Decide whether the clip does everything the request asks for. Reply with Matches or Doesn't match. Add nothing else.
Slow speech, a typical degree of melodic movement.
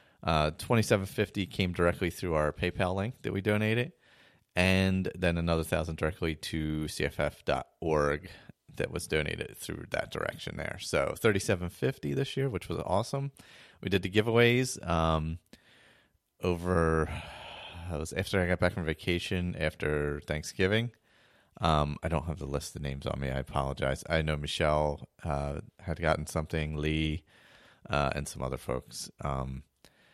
Doesn't match